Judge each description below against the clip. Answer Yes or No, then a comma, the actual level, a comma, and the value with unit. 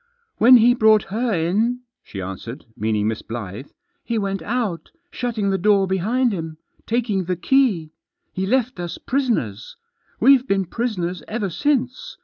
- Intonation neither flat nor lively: No, wide, 6.6 semitones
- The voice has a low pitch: No, high, 200 Hz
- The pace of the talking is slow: No, average, 160 wpm